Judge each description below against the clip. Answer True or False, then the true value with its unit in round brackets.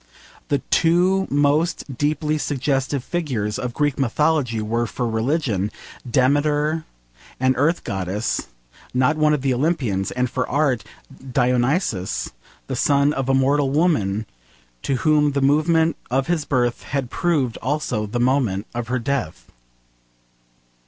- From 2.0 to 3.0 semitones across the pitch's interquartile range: False (3.8 semitones)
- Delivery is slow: True (130 wpm)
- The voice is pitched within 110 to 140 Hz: True (135 Hz)